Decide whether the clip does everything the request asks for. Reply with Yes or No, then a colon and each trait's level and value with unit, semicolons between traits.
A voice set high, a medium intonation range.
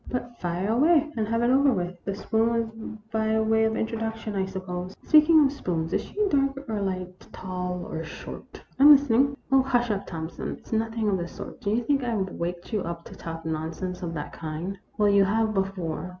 Yes: high, 215 Hz; average, 4.6 semitones